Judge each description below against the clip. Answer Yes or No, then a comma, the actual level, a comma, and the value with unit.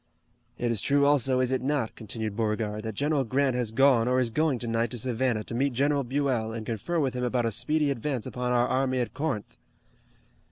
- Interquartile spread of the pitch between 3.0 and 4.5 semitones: Yes, average, 3.3 semitones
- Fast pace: Yes, fast, 210 wpm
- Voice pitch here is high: No, low, 125 Hz